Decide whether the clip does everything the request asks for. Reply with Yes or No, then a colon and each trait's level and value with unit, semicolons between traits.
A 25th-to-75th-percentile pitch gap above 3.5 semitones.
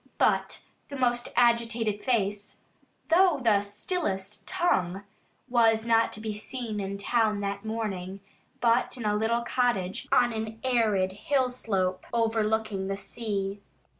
No: average, 3.0 semitones